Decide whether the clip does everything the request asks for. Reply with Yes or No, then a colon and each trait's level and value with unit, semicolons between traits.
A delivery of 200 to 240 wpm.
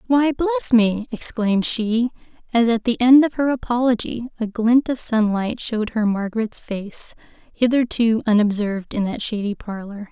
No: average, 155 wpm